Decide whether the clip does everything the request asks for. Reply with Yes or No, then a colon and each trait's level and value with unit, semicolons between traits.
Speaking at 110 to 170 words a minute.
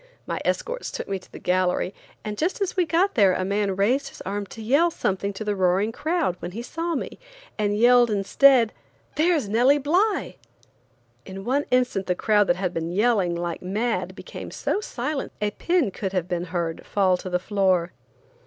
No: average, 195 wpm